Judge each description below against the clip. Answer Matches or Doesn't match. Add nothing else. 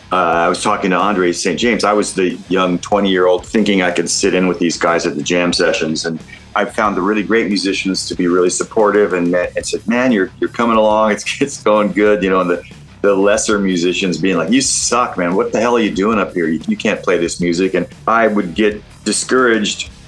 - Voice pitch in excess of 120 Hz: Doesn't match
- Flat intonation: Doesn't match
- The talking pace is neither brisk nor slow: Doesn't match